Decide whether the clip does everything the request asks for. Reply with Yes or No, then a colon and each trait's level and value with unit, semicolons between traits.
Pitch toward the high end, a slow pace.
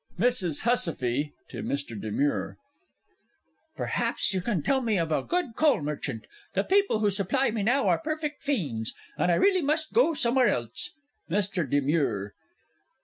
No: high, 200 Hz; average, 160 wpm